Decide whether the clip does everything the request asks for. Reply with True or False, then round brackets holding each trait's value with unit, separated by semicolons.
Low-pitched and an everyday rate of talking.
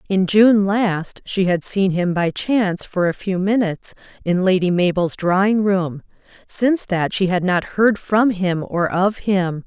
False (190 Hz; 180 wpm)